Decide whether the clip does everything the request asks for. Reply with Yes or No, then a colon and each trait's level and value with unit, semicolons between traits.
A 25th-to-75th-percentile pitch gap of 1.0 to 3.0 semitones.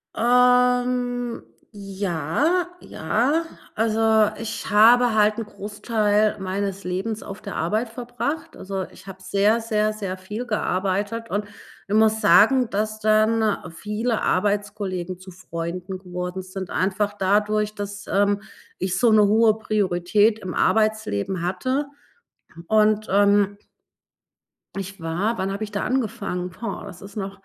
Yes: narrow, 2.5 semitones